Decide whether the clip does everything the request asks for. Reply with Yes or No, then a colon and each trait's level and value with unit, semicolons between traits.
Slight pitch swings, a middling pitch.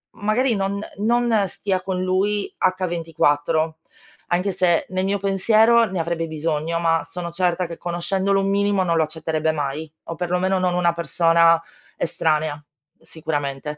No: average, 3.2 semitones; medium, 175 Hz